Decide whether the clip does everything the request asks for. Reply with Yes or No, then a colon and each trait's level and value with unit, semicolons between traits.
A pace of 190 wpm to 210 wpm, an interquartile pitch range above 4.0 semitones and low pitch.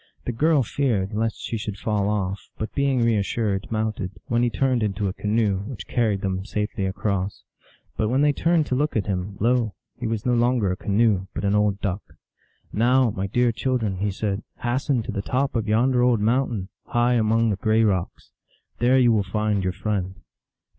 No: average, 200 wpm; average, 3.4 semitones; low, 110 Hz